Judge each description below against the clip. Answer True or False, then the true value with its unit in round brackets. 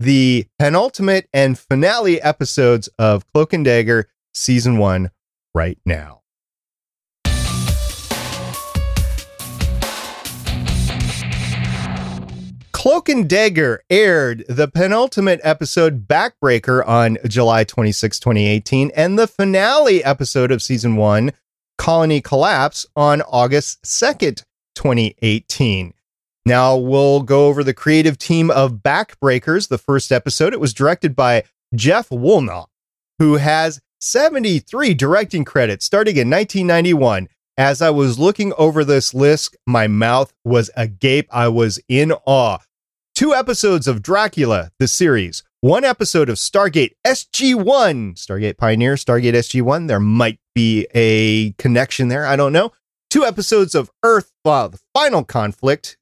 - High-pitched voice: False (135 Hz)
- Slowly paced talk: True (125 wpm)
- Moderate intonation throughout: False (6.0 semitones)